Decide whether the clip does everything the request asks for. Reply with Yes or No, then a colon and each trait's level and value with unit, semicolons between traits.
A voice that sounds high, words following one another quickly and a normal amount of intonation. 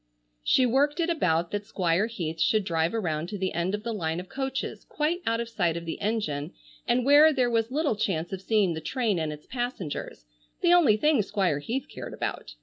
No: high, 210 Hz; fast, 210 wpm; wide, 6.9 semitones